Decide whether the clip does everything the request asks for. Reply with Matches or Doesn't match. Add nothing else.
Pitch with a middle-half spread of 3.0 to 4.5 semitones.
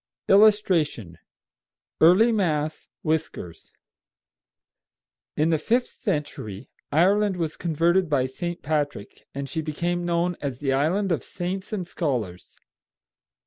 Matches